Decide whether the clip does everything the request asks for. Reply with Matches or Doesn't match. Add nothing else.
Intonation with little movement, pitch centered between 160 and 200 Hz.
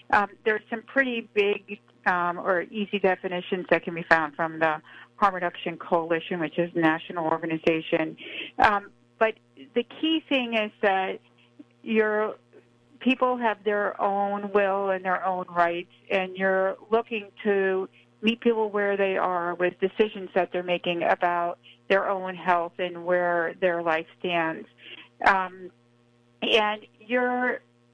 Doesn't match